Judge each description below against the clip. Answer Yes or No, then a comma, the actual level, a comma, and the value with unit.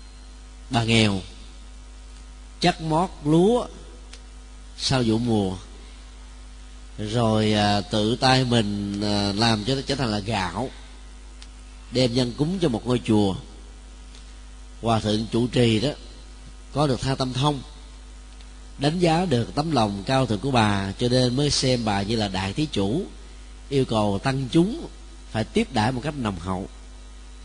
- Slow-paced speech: Yes, slow, 150 wpm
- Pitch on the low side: Yes, low, 105 Hz